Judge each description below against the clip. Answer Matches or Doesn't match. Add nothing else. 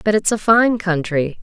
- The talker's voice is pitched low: Doesn't match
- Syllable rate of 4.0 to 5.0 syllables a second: Matches